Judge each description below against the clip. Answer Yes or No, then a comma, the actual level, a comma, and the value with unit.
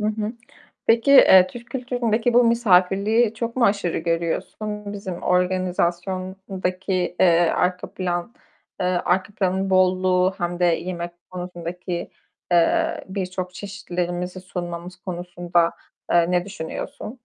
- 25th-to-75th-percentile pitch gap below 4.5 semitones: Yes, narrow, 2.6 semitones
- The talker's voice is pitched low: No, medium, 185 Hz